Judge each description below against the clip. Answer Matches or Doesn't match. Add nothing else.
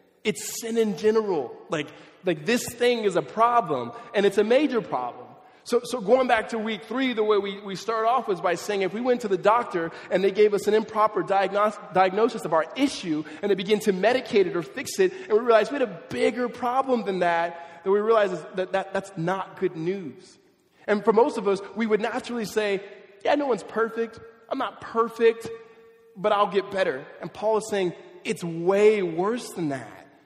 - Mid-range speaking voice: Doesn't match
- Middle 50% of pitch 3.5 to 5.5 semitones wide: Doesn't match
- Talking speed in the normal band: Doesn't match